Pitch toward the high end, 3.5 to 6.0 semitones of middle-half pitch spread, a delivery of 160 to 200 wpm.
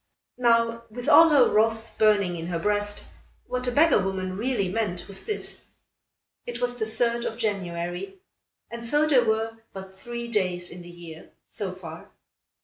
Yes: high, 220 Hz; average, 4.2 semitones; average, 165 wpm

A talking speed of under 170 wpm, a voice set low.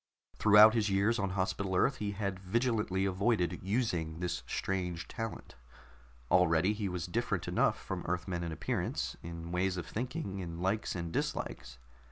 Yes: average, 155 wpm; very low, 95 Hz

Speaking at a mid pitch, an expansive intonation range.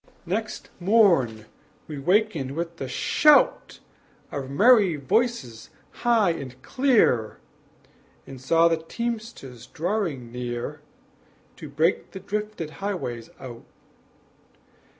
Yes: medium, 165 Hz; wide, 8.3 semitones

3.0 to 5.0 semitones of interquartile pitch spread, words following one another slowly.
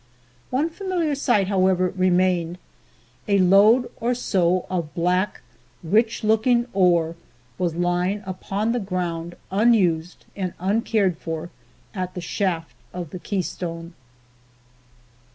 Yes: average, 3.5 semitones; slow, 115 wpm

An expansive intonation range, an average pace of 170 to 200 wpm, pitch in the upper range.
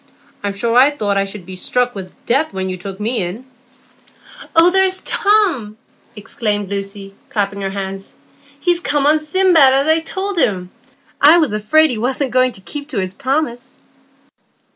Yes: wide, 7.5 semitones; average, 175 wpm; high, 245 Hz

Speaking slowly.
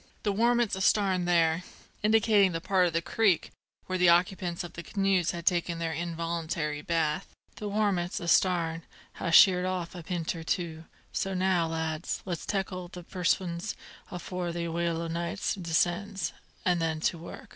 No: average, 165 wpm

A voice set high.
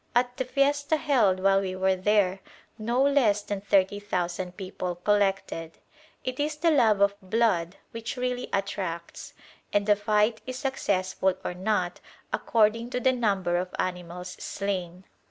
Yes: high, 205 Hz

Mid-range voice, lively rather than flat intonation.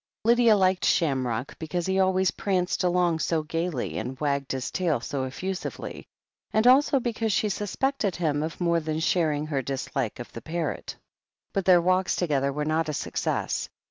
No: medium, 170 Hz; average, 4.6 semitones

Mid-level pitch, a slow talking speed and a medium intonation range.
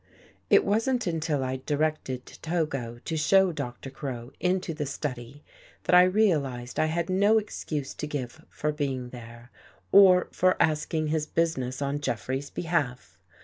No: medium, 150 Hz; average, 145 wpm; average, 4.6 semitones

